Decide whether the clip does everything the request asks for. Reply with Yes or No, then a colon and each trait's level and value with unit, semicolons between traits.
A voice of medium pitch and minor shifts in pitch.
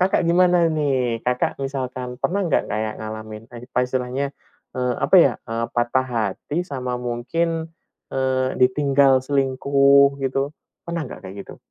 No: low, 130 Hz; narrow, 2.3 semitones